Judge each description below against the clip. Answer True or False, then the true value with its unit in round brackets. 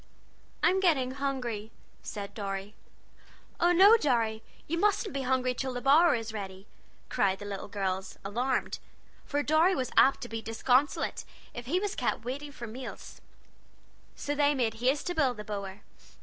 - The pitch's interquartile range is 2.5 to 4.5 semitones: False (5.2 semitones)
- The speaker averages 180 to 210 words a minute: False (165 wpm)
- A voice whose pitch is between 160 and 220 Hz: False (255 Hz)